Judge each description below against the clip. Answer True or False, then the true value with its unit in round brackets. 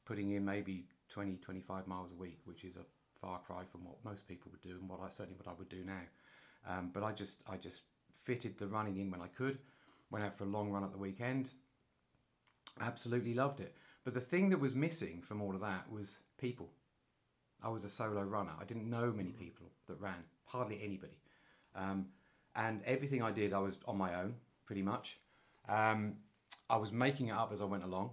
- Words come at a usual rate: False (215 wpm)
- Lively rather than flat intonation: False (4.0 semitones)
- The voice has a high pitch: False (100 Hz)